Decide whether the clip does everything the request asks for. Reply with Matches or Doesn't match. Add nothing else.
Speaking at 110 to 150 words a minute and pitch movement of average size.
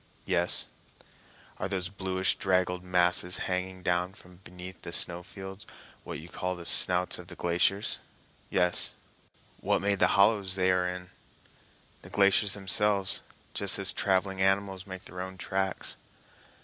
Doesn't match